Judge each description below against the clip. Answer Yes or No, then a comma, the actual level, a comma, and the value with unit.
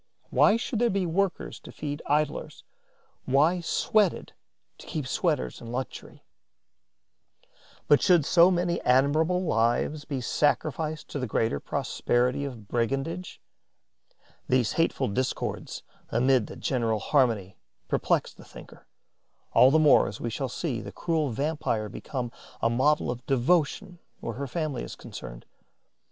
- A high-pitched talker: No, medium, 140 Hz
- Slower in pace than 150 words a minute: Yes, slow, 135 wpm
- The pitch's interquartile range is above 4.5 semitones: Yes, average, 5.1 semitones